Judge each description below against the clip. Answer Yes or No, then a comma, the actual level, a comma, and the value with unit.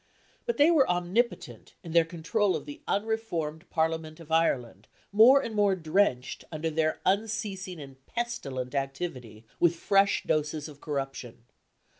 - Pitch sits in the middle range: Yes, medium, 165 Hz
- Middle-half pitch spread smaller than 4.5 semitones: No, wide, 5.5 semitones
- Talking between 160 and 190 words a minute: No, average, 140 wpm